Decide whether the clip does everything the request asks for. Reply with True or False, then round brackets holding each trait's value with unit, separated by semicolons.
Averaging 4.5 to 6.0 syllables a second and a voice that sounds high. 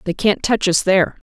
True (5.5 syllables/s; 195 Hz)